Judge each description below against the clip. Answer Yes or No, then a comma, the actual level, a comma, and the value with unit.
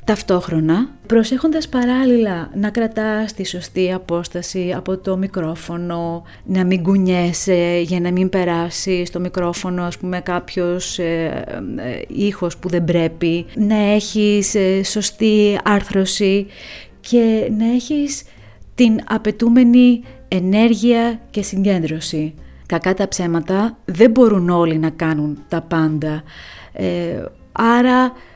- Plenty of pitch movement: No, average, 4.0 semitones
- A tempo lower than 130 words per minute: Yes, slow, 115 wpm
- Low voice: No, high, 190 Hz